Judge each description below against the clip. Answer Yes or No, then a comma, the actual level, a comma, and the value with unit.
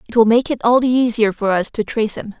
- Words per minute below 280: No, fast, 300 wpm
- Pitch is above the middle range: Yes, high, 230 Hz